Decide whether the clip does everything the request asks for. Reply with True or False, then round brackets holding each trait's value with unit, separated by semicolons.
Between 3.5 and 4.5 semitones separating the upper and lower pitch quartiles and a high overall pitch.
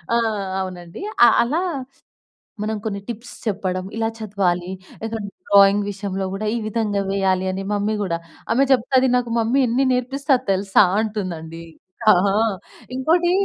True (3.8 semitones; 205 Hz)